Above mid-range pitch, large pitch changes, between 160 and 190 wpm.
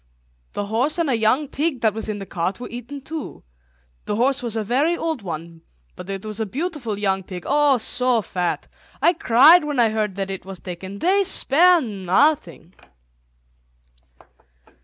Yes: high, 230 Hz; wide, 6.9 semitones; average, 175 wpm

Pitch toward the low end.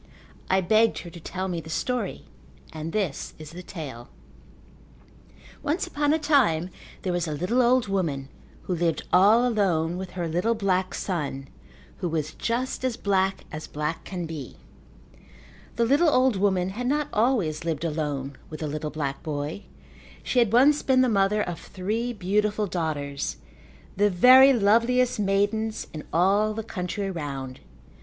No: high, 190 Hz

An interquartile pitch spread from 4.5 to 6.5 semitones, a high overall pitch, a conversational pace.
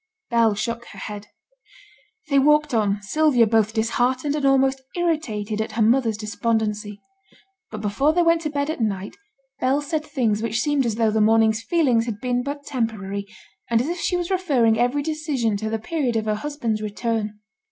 Yes: average, 5.0 semitones; high, 235 Hz; average, 185 wpm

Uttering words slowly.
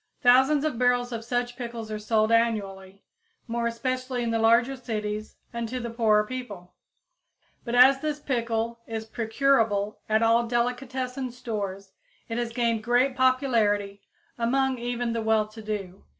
No: average, 150 wpm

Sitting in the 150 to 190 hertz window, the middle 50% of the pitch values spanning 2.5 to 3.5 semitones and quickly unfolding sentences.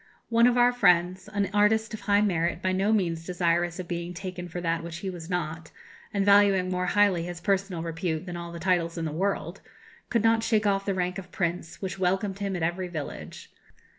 Yes: medium, 185 Hz; average, 2.8 semitones; fast, 215 wpm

